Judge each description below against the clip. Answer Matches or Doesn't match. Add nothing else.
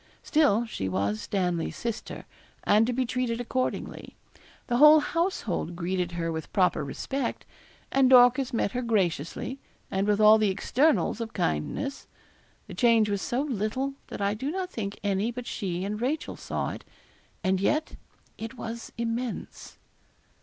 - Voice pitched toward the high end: Matches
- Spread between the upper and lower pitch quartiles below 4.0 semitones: Doesn't match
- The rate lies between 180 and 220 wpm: Doesn't match